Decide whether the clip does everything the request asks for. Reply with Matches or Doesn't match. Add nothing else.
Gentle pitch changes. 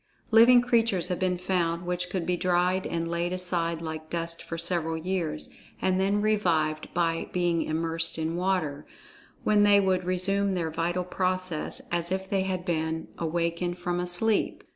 Matches